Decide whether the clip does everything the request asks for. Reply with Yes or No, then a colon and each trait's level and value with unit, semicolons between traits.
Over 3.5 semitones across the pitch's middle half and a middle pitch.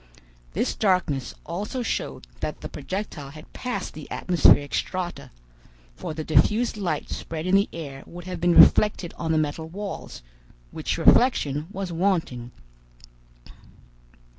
Yes: average, 4.1 semitones; medium, 175 Hz